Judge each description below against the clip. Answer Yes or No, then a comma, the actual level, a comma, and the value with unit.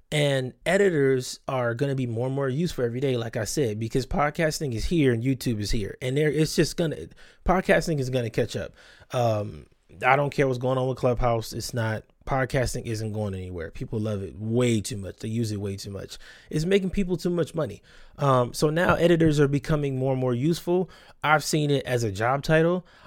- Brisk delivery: Yes, fast, 215 wpm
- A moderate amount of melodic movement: Yes, average, 4.7 semitones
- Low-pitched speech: Yes, low, 130 Hz